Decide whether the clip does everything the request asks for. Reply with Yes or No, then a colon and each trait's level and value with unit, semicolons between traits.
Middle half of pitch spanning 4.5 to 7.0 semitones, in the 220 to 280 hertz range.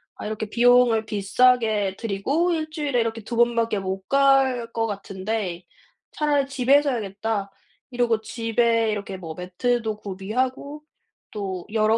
No: average, 3.7 semitones; high, 225 Hz